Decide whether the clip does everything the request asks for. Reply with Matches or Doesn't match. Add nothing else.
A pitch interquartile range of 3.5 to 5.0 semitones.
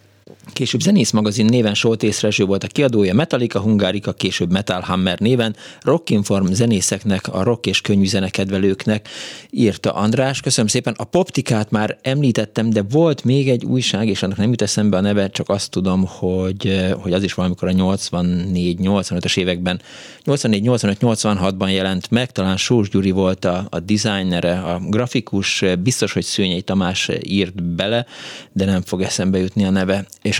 Doesn't match